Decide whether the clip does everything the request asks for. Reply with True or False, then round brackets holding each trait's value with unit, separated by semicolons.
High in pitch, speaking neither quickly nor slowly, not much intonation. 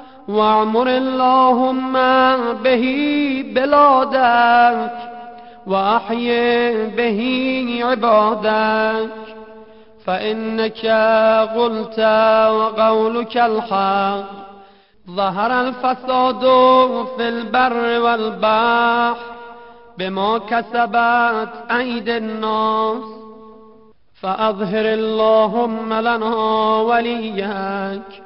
False (230 Hz; 50 wpm; 1.5 semitones)